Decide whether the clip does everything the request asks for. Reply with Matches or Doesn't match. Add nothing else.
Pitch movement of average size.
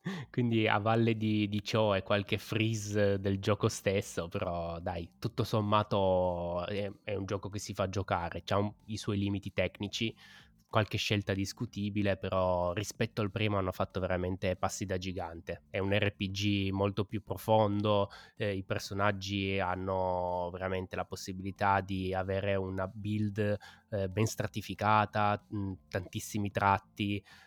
Doesn't match